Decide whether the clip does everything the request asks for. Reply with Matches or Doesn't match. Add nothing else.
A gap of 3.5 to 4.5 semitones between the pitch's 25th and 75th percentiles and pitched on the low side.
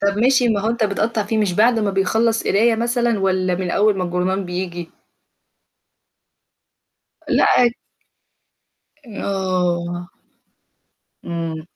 Doesn't match